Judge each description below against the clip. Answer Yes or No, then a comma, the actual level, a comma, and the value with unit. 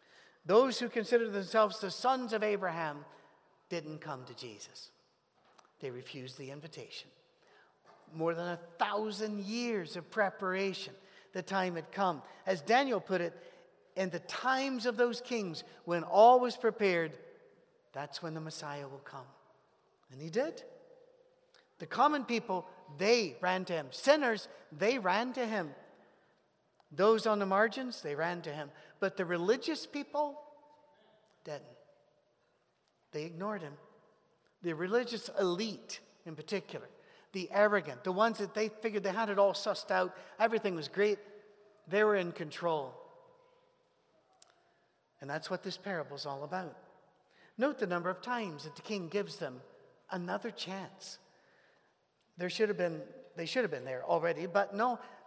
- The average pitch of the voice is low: No, high, 200 Hz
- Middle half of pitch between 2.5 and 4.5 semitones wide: No, average, 5.3 semitones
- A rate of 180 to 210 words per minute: No, average, 145 wpm